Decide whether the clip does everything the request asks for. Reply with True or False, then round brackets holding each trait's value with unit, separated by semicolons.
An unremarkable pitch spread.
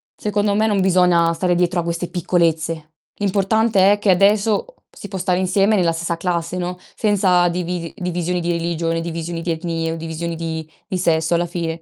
False (2.2 semitones)